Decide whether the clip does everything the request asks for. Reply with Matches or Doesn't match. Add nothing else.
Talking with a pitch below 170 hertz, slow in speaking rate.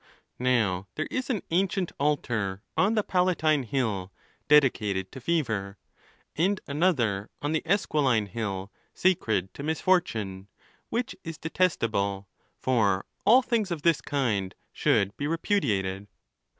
Matches